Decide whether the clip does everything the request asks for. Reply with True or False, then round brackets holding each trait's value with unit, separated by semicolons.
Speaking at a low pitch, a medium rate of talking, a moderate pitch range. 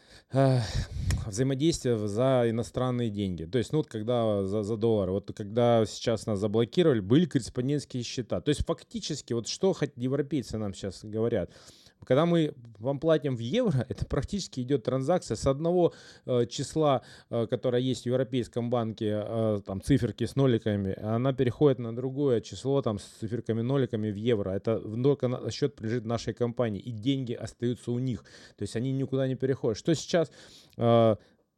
False (120 Hz; 165 wpm; 3.4 semitones)